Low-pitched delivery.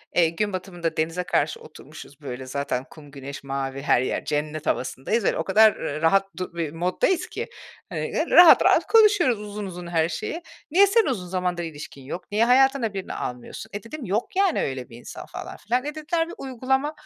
No: medium, 185 Hz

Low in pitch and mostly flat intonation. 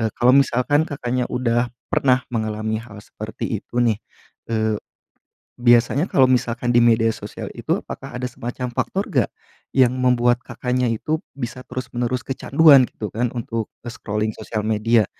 Yes: low, 120 Hz; narrow, 2.0 semitones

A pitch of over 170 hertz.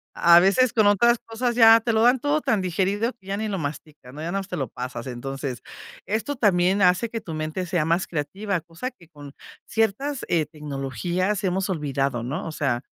Yes: medium, 185 Hz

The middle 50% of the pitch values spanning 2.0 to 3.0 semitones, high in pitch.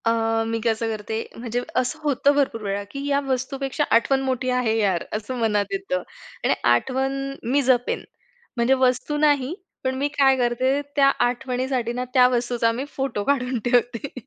Yes: narrow, 2.5 semitones; very high, 255 Hz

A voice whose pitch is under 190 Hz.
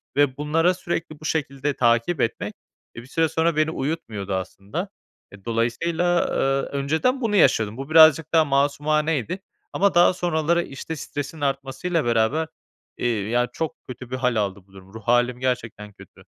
Yes: medium, 140 Hz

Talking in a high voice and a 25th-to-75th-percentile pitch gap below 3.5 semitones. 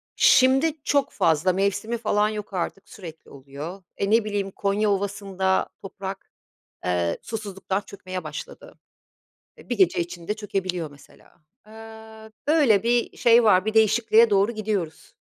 Yes: high, 200 Hz; average, 3.1 semitones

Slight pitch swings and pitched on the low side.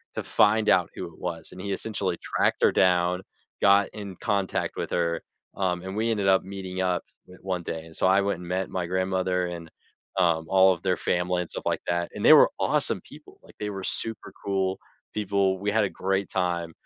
Yes: narrow, 1.9 semitones; very low, 95 Hz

